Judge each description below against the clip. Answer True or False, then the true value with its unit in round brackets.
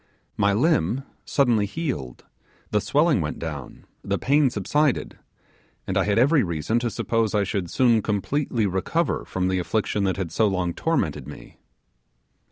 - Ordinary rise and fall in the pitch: False (6.0 semitones)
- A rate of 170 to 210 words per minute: False (155 wpm)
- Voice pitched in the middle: False (105 Hz)